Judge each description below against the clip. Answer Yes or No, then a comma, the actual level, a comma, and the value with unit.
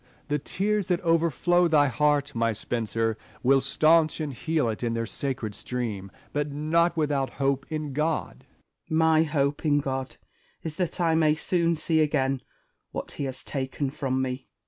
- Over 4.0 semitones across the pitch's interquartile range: No, average, 3.4 semitones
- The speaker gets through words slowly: No, average, 170 wpm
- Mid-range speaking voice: Yes, medium, 145 Hz